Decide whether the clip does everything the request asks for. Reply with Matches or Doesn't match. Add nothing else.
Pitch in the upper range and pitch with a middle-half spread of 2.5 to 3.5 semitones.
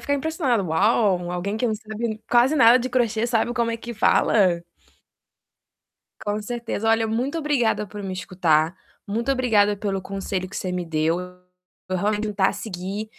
Doesn't match